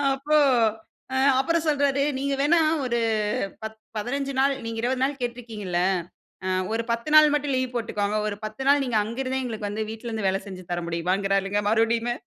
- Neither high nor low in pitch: No, high, 235 Hz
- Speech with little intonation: No, average, 4.5 semitones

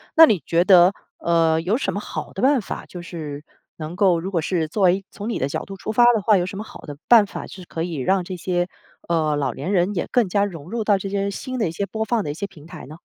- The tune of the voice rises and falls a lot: No, average, 3.6 semitones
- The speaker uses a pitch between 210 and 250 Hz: No, medium, 185 Hz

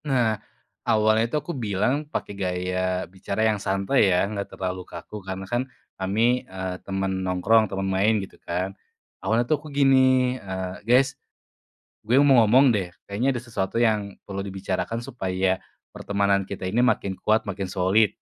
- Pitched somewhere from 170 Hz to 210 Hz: No, low, 100 Hz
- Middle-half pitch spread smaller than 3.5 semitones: No, average, 4.1 semitones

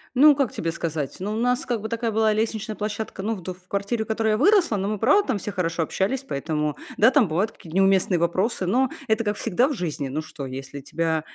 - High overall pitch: Yes, high, 205 Hz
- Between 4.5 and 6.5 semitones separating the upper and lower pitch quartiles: Yes, average, 5.3 semitones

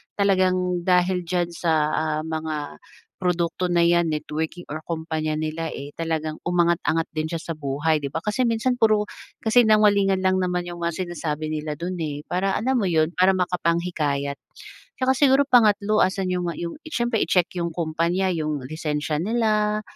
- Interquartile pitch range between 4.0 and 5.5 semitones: No, average, 3.4 semitones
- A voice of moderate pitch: Yes, medium, 175 Hz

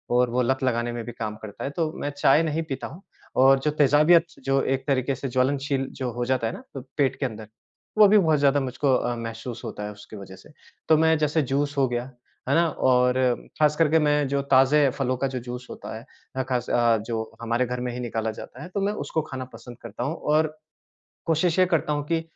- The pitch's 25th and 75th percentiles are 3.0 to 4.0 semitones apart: Yes, average, 3.6 semitones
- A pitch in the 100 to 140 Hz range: Yes, low, 135 Hz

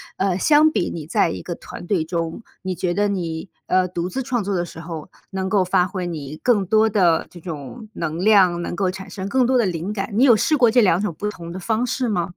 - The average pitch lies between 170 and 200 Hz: Yes, high, 190 Hz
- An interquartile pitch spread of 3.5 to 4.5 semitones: Yes, average, 3.9 semitones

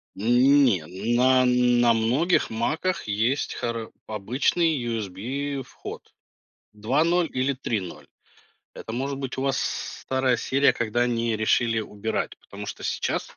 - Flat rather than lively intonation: No, average, 3.5 semitones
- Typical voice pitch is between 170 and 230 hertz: No, low, 125 Hz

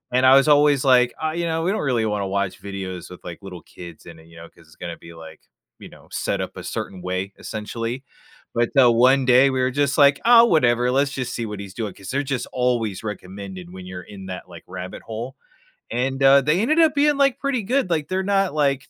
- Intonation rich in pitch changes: Yes, wide, 7.1 semitones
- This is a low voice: Yes, low, 120 Hz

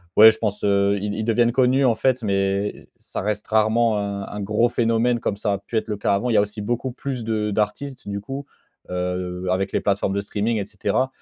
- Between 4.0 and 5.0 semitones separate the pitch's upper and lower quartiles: No, average, 2.7 semitones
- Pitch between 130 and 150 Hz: No, low, 105 Hz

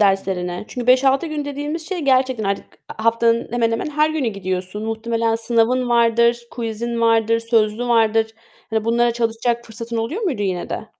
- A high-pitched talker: Yes, high, 230 Hz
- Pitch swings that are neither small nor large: No, narrow, 2.0 semitones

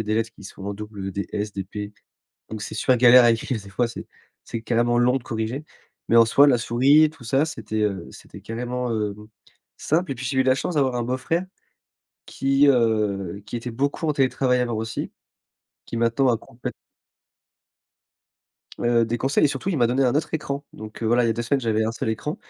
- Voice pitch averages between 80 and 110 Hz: No, low, 120 Hz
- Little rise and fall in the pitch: No, average, 3.3 semitones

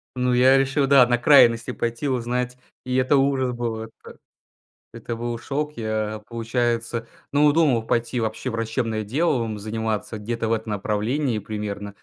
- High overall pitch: No, low, 120 Hz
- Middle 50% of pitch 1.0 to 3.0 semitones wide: Yes, narrow, 2.6 semitones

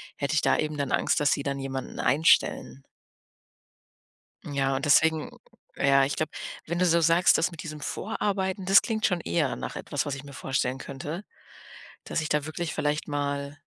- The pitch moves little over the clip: No, average, 3.1 semitones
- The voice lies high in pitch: No, medium, 150 Hz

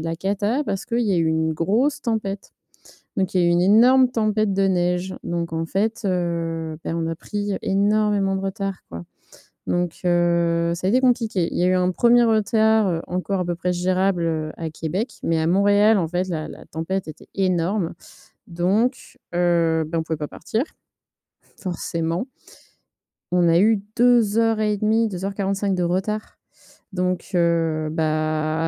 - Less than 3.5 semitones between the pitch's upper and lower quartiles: No, average, 3.8 semitones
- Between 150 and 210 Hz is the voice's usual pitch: Yes, medium, 185 Hz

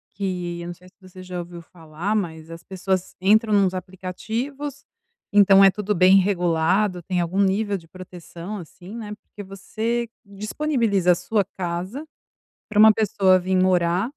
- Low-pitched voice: No, high, 190 Hz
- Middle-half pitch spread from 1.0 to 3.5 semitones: Yes, average, 2.9 semitones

